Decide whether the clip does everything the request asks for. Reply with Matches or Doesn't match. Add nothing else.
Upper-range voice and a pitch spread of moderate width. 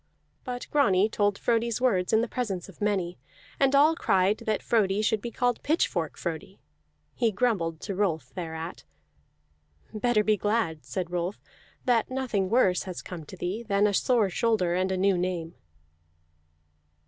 Matches